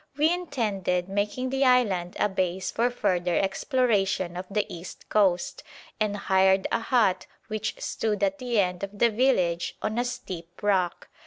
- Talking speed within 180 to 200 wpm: No, average, 160 wpm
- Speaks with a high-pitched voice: Yes, high, 200 Hz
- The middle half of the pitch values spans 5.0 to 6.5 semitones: No, average, 4.3 semitones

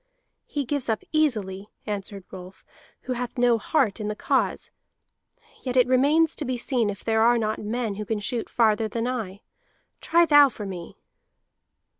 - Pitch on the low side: No, high, 230 Hz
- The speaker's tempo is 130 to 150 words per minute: No, average, 170 wpm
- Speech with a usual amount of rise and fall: Yes, average, 3.6 semitones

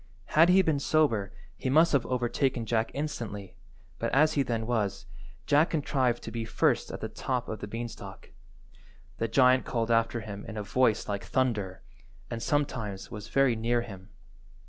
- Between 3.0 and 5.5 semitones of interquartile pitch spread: Yes, average, 3.8 semitones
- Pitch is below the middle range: Yes, low, 120 Hz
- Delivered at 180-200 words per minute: No, average, 170 wpm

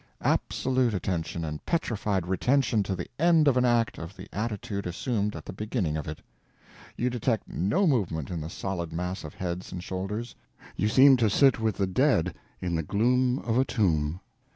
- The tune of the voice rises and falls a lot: Yes, wide, 5.8 semitones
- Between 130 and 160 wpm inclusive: No, average, 185 wpm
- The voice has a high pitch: No, low, 100 Hz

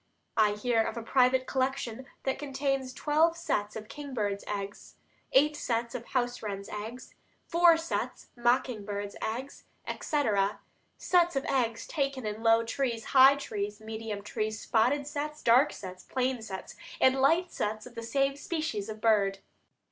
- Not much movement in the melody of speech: No, average, 4.2 semitones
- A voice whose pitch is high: Yes, high, 245 Hz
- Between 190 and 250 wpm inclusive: No, average, 155 wpm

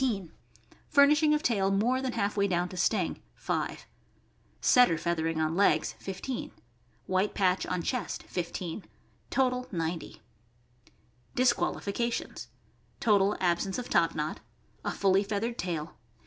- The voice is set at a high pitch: Yes, high, 195 Hz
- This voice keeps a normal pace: No, slow, 125 wpm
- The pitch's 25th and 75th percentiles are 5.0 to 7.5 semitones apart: Yes, wide, 5.5 semitones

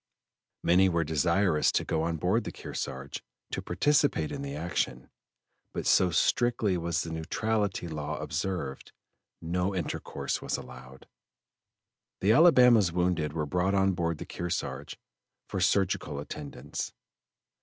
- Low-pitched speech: Yes, very low, 90 Hz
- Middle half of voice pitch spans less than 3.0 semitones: No, average, 3.9 semitones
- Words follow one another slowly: Yes, slow, 130 wpm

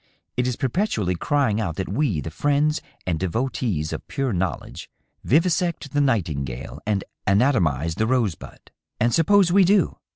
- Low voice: Yes, low, 115 Hz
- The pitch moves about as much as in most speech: No, wide, 8.4 semitones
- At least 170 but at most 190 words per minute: No, average, 150 wpm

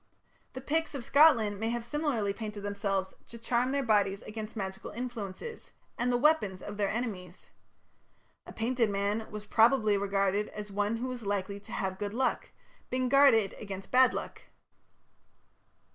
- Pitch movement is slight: No, average, 3.7 semitones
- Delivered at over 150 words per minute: Yes, average, 160 wpm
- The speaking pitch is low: No, high, 215 Hz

